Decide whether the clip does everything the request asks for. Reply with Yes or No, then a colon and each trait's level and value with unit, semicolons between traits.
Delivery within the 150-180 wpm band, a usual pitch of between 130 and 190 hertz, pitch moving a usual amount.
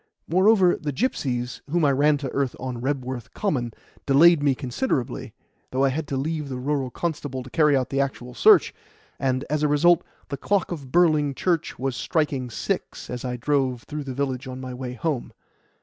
No: average, 190 wpm; medium, 140 Hz; average, 3.0 semitones